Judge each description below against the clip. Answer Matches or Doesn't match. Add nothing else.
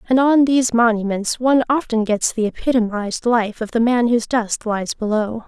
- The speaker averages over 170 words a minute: Matches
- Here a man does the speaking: Doesn't match